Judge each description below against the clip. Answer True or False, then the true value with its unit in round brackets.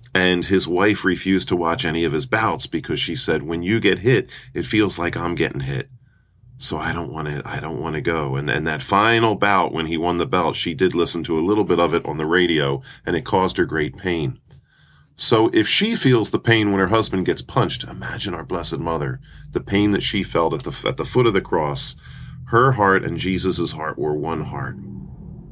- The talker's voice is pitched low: True (90 Hz)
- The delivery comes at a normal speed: False (230 wpm)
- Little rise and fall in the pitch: False (4.3 semitones)